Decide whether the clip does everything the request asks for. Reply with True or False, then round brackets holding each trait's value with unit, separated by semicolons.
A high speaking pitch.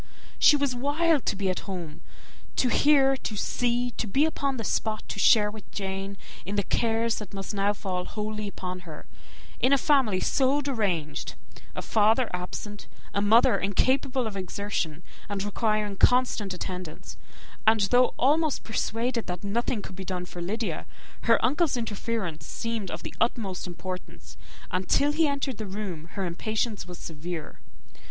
True (210 Hz)